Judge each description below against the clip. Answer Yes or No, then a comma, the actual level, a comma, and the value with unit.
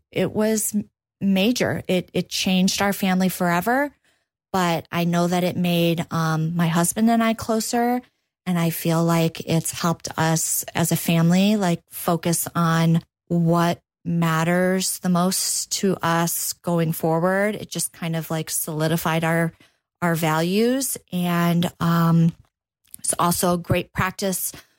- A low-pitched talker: No, medium, 175 Hz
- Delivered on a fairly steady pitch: Yes, narrow, 2.1 semitones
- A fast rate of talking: No, average, 140 wpm